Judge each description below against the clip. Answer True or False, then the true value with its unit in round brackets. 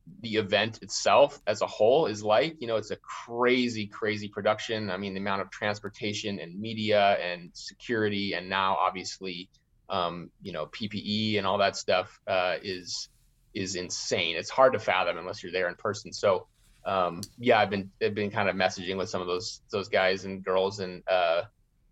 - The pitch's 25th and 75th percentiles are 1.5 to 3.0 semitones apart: True (2.4 semitones)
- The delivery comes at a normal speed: True (190 wpm)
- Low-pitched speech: True (100 Hz)